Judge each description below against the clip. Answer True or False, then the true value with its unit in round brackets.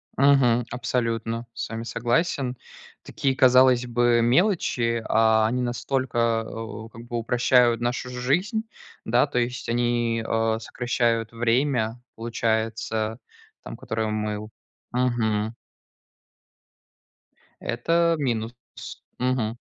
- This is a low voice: True (120 Hz)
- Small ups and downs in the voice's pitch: True (1.8 semitones)